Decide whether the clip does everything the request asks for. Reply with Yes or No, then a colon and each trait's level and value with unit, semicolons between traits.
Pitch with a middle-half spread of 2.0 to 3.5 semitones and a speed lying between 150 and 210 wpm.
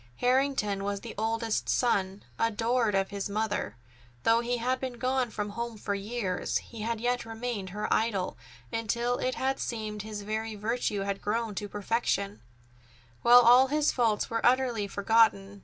Yes: average, 2.9 semitones; average, 160 wpm